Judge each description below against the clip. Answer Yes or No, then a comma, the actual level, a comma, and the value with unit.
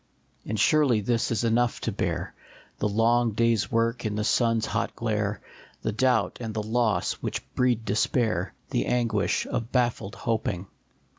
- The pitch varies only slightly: Yes, narrow, 1.9 semitones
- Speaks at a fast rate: No, average, 170 wpm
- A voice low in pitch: Yes, low, 115 Hz